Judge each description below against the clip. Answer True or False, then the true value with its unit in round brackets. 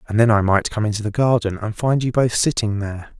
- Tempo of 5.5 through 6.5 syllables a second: True (6.0 syllables/s)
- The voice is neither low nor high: False (110 Hz)